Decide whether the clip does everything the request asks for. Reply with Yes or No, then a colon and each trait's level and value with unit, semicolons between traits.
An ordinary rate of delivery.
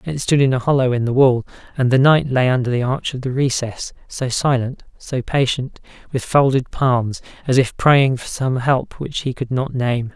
No: fast, 215 wpm